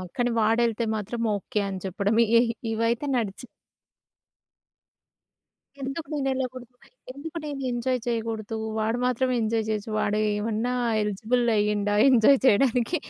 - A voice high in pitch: Yes, high, 230 Hz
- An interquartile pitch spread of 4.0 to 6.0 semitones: No, average, 2.8 semitones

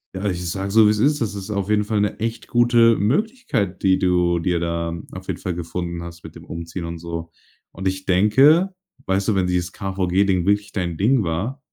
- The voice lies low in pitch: Yes, very low, 95 Hz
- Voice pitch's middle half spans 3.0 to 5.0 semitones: Yes, average, 3.6 semitones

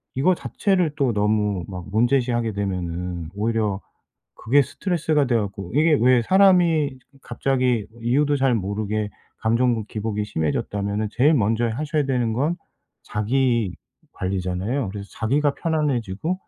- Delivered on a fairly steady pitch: No, wide, 5.5 semitones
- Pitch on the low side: Yes, low, 115 Hz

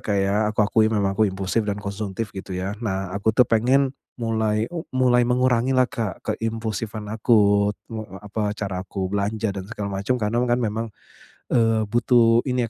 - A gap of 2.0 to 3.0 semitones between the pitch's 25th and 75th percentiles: Yes, narrow, 2.6 semitones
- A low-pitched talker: Yes, low, 110 Hz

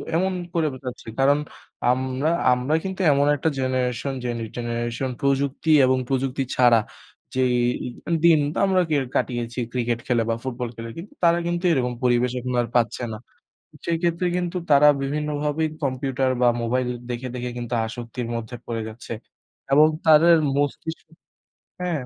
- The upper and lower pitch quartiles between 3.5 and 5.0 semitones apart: Yes, average, 3.8 semitones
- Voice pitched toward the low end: Yes, low, 130 Hz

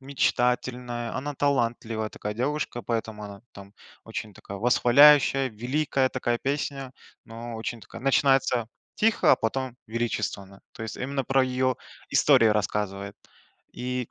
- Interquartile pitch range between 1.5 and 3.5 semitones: Yes, average, 3.2 semitones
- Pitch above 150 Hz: No, low, 120 Hz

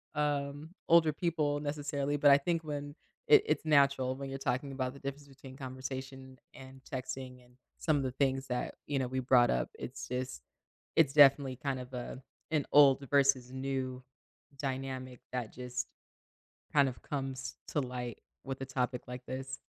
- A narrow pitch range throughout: Yes, narrow, 1.8 semitones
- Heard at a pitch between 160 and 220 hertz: No, low, 135 Hz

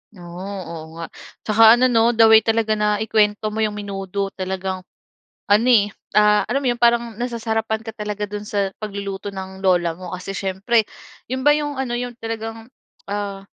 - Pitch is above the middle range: Yes, high, 210 Hz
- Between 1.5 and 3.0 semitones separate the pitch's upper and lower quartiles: Yes, narrow, 2.6 semitones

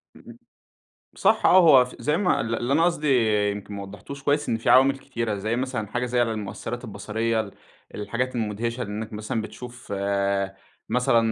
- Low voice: Yes, low, 115 Hz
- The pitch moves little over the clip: No, average, 3.2 semitones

